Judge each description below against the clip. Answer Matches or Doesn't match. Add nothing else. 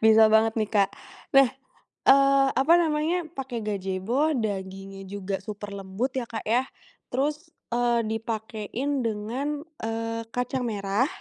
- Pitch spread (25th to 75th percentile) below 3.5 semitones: Doesn't match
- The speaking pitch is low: Doesn't match